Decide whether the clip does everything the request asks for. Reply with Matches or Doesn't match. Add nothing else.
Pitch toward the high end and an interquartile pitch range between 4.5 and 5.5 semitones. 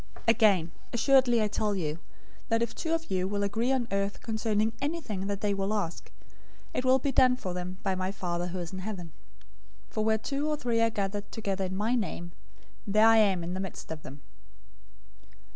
Doesn't match